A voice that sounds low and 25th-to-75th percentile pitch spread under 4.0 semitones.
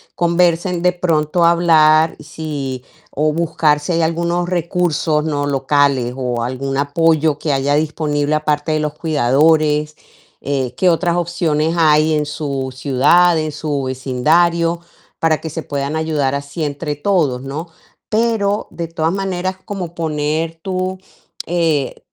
No: medium, 155 Hz; average, 2.9 semitones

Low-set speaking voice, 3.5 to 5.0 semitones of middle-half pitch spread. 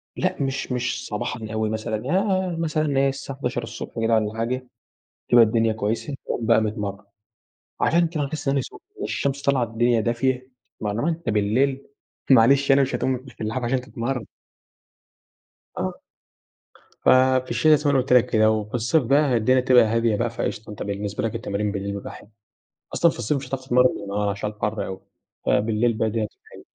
Yes: low, 120 Hz; average, 3.8 semitones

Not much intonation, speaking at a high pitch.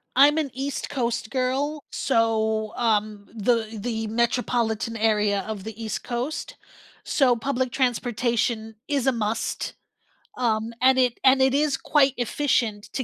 No: average, 3.1 semitones; high, 235 Hz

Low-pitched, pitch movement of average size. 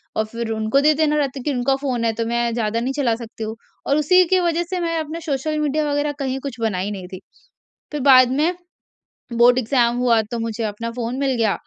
No: very high, 250 Hz; average, 4.3 semitones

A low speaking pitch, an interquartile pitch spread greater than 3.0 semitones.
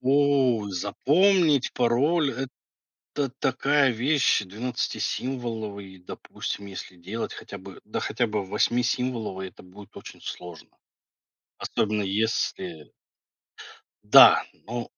Yes: low, 115 Hz; average, 5.0 semitones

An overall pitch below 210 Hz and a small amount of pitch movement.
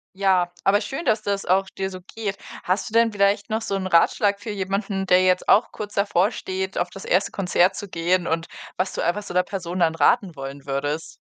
Yes: high, 190 Hz; narrow, 2.3 semitones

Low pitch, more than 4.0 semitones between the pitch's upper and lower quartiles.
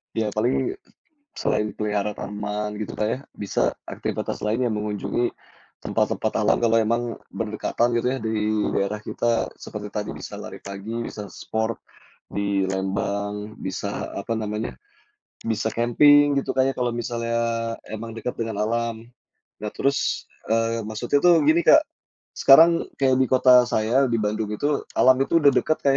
No: low, 115 Hz; average, 3.0 semitones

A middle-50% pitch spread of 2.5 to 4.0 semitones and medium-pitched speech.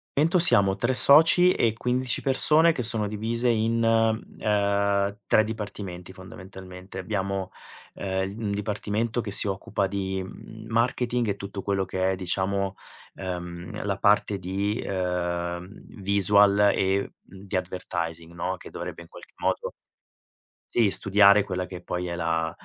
No: average, 2.9 semitones; low, 100 Hz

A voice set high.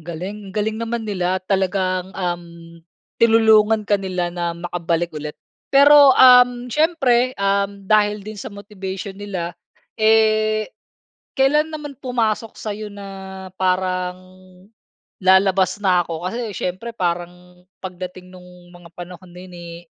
Yes: high, 195 Hz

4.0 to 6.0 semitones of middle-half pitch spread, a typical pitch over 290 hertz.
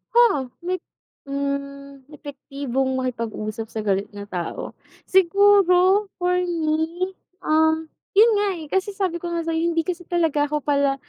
Yes: average, 4.5 semitones; very high, 315 Hz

